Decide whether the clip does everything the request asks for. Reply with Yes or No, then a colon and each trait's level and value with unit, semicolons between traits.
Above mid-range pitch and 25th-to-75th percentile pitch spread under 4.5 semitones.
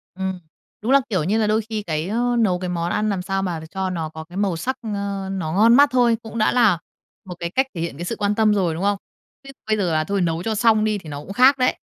Yes: high, 200 Hz; average, 3.9 semitones